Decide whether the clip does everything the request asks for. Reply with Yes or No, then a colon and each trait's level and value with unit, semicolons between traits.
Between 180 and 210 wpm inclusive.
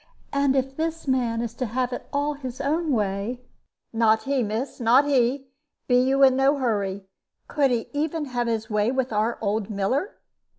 Yes: average, 185 wpm